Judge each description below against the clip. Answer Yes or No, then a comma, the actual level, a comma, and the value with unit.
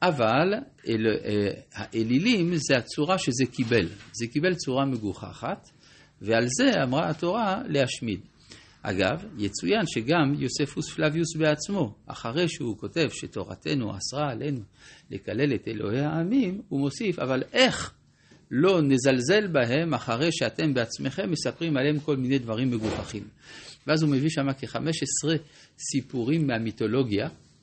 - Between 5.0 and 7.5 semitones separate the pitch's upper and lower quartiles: Yes, average, 5.3 semitones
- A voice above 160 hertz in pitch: No, medium, 140 Hz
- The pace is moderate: Yes, average, 120 wpm